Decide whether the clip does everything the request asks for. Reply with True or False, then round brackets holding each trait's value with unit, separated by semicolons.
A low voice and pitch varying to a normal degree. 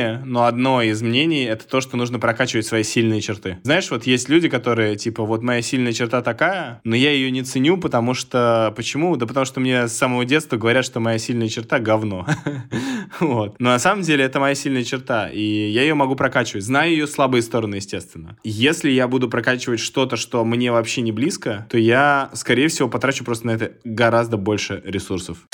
True (120 Hz; 3.0 semitones)